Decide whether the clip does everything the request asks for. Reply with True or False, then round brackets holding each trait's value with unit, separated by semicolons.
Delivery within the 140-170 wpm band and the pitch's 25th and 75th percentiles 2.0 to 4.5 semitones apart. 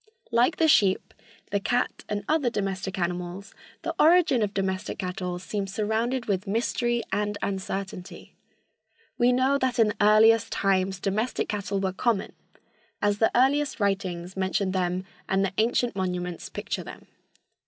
True (145 wpm; 3.7 semitones)